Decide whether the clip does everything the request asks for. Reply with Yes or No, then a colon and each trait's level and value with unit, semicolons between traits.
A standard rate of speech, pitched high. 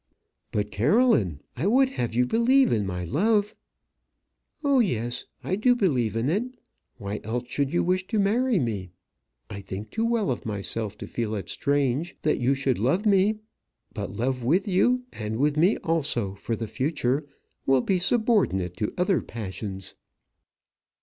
No: average, 165 wpm; low, 135 Hz